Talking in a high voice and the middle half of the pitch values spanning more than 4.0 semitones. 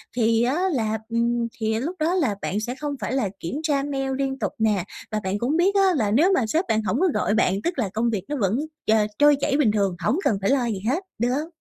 Yes: high, 240 Hz; average, 5.1 semitones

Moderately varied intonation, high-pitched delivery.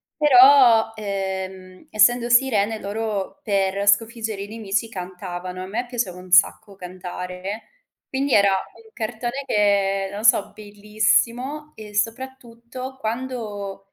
Yes: average, 3.5 semitones; high, 215 Hz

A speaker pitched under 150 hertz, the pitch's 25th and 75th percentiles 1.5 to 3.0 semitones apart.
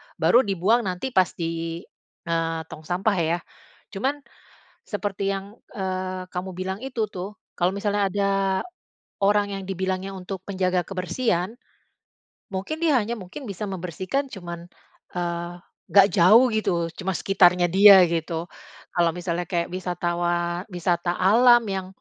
No: medium, 185 Hz; narrow, 2.4 semitones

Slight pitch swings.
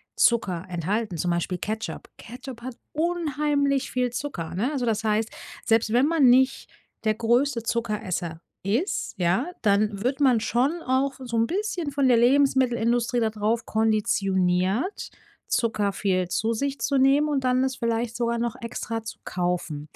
No: average, 4.0 semitones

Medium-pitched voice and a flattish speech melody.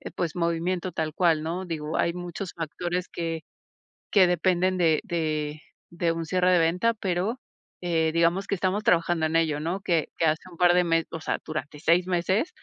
Yes: medium, 170 Hz; narrow, 1.9 semitones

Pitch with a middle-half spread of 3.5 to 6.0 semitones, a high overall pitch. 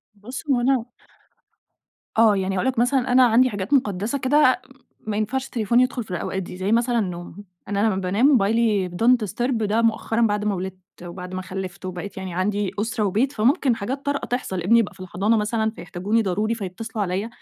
Yes: average, 4.0 semitones; high, 215 Hz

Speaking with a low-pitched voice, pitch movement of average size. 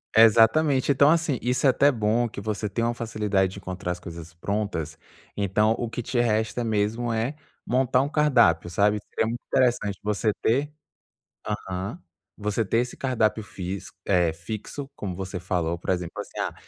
Yes: low, 110 Hz; average, 4.1 semitones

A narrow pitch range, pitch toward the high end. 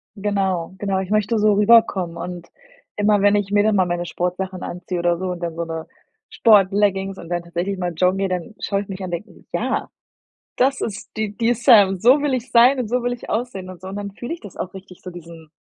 No: average, 3.1 semitones; high, 195 Hz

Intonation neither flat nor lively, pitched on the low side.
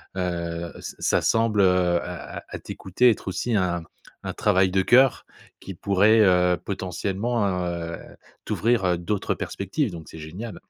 Yes: average, 3.2 semitones; very low, 95 Hz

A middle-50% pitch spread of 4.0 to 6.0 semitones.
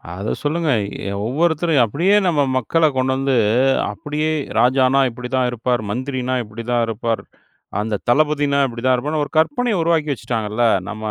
Yes: average, 4.4 semitones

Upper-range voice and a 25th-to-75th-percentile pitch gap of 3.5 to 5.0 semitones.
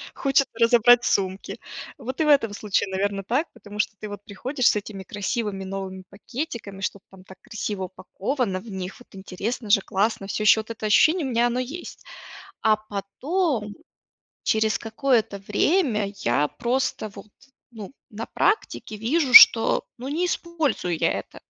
Yes: high, 215 Hz; average, 4.3 semitones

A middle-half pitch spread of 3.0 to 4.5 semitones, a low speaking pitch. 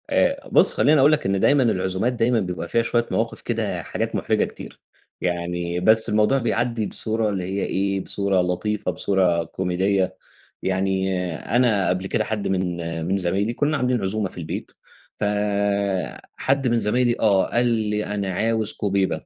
Yes: average, 3.4 semitones; low, 100 Hz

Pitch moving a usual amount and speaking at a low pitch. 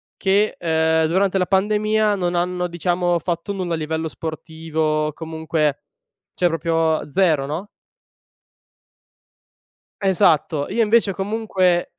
No: average, 3.2 semitones; medium, 175 Hz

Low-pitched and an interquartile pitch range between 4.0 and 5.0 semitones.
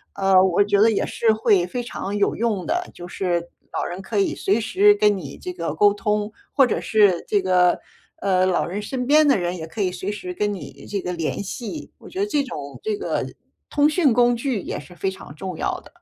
No: high, 205 Hz; average, 4.6 semitones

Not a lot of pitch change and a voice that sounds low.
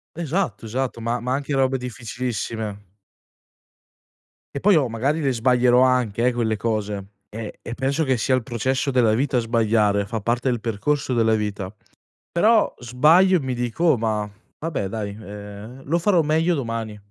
No: average, 3.7 semitones; low, 120 Hz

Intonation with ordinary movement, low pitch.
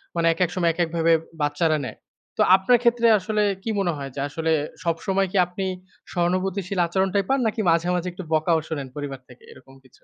No: average, 3.2 semitones; medium, 175 Hz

